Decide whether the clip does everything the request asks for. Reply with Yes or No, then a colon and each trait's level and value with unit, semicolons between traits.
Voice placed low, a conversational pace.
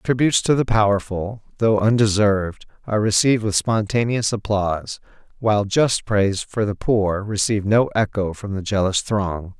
Yes: low, 105 Hz; average, 150 wpm